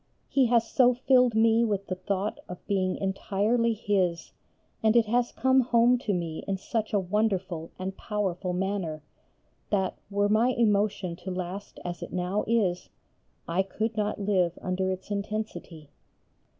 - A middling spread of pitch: Yes, average, 3.3 semitones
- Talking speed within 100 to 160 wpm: Yes, average, 155 wpm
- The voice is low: No, high, 200 Hz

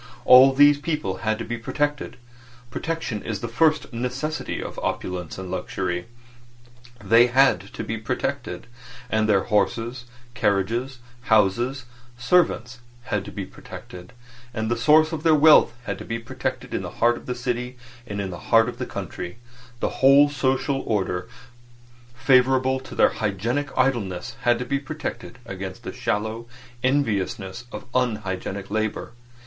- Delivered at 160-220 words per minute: No, average, 150 wpm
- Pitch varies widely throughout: No, average, 4.3 semitones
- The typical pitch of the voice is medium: No, low, 120 Hz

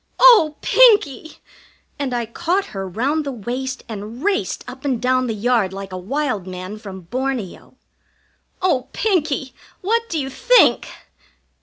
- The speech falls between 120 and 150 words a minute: Yes, average, 145 wpm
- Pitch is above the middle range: Yes, very high, 255 Hz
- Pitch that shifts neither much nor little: No, wide, 6.4 semitones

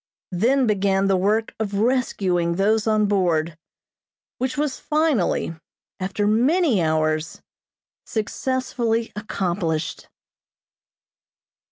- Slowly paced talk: Yes, slow, 85 wpm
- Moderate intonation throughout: Yes, average, 4.8 semitones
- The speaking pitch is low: No, high, 205 Hz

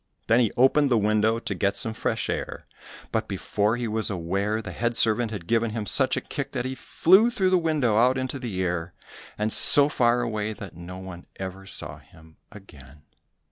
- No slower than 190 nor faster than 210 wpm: Yes, average, 200 wpm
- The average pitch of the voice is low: Yes, low, 110 Hz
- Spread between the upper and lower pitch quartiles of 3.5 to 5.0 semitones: Yes, average, 4.3 semitones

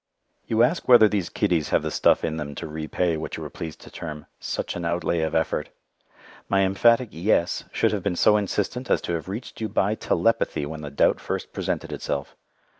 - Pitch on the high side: No, very low, 90 Hz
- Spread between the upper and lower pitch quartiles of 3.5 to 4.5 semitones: No, average, 5.1 semitones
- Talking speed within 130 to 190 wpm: No, fast, 205 wpm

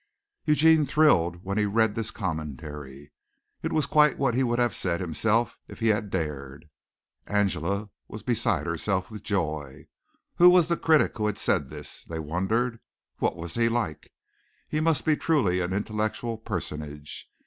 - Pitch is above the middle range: No, low, 105 Hz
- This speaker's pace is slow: No, average, 160 wpm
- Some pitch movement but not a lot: No, wide, 6.5 semitones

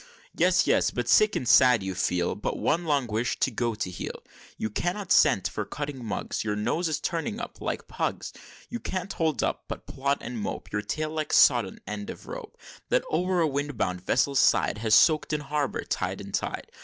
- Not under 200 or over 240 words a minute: Yes, fast, 205 wpm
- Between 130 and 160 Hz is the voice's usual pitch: Yes, low, 135 Hz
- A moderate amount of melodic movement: No, wide, 6.7 semitones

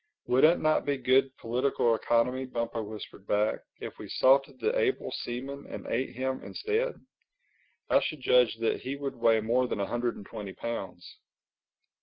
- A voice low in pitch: Yes, low, 125 Hz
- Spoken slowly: No, average, 170 wpm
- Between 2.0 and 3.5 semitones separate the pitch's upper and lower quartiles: Yes, average, 3.1 semitones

